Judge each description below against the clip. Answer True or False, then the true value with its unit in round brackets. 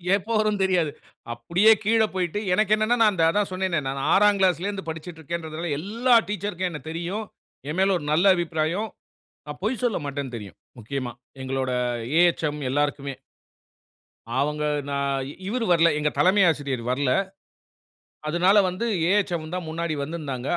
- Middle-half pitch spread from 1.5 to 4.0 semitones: False (5.3 semitones)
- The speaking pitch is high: False (170 Hz)